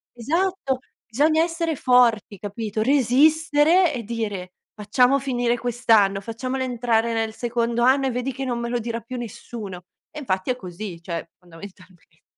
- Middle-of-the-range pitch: No, high, 235 Hz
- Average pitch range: Yes, average, 3.9 semitones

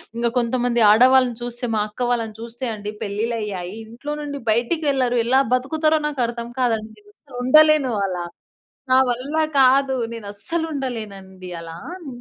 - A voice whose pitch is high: Yes, high, 240 Hz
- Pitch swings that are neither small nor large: Yes, average, 3.4 semitones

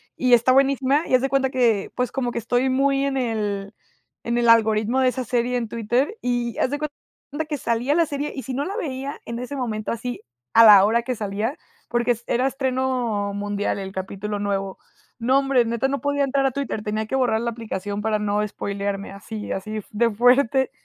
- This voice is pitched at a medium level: No, high, 240 Hz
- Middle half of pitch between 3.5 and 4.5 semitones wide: Yes, average, 3.9 semitones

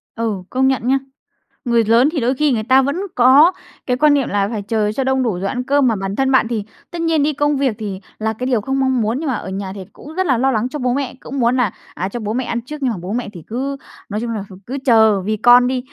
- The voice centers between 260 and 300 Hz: No, high, 245 Hz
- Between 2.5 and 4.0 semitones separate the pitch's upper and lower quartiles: Yes, average, 3.7 semitones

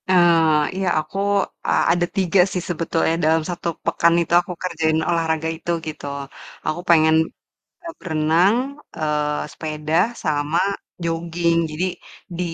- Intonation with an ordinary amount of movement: No, narrow, 1.8 semitones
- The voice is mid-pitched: Yes, medium, 165 Hz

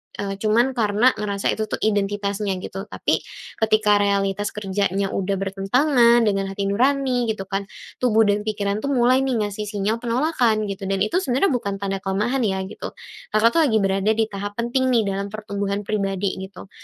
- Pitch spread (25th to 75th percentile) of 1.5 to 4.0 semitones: Yes, average, 2.8 semitones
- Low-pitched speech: No, high, 205 Hz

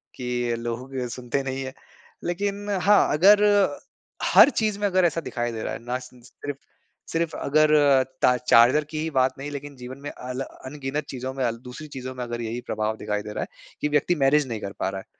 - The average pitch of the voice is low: Yes, low, 130 Hz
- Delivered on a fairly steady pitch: No, average, 3.9 semitones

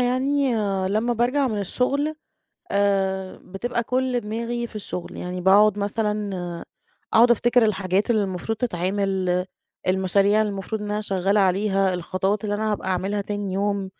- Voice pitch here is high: Yes, high, 205 Hz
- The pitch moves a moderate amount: Yes, average, 3.2 semitones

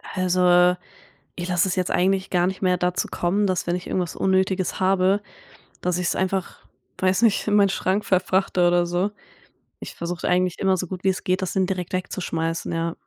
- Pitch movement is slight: Yes, narrow, 1.1 semitones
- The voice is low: No, medium, 185 Hz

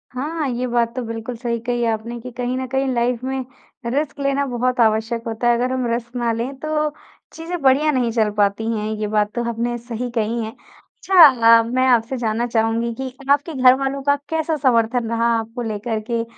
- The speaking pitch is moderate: No, high, 240 Hz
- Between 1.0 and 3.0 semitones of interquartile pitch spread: Yes, narrow, 2.5 semitones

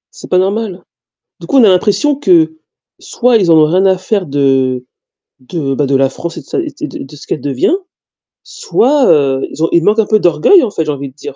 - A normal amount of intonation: No, wide, 7.9 semitones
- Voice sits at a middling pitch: Yes, medium, 180 Hz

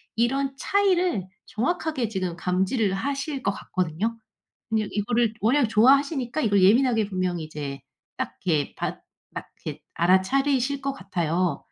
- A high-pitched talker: Yes, high, 220 Hz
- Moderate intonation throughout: No, wide, 6.6 semitones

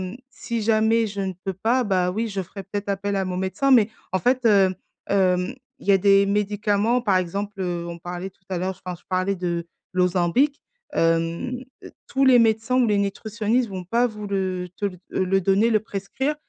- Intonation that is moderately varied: Yes, average, 3.1 semitones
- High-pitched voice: Yes, high, 200 Hz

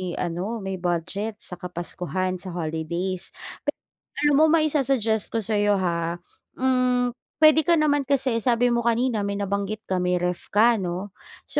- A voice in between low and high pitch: No, high, 205 Hz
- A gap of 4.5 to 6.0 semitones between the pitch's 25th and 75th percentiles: Yes, wide, 5.6 semitones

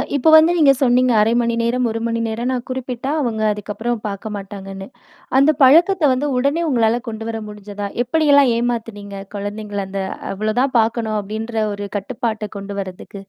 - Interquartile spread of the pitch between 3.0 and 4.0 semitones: Yes, average, 3.7 semitones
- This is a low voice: No, high, 225 Hz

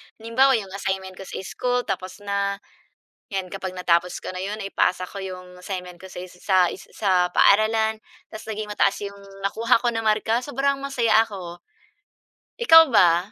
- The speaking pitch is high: Yes, high, 200 Hz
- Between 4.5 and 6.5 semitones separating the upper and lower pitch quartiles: No, average, 3.3 semitones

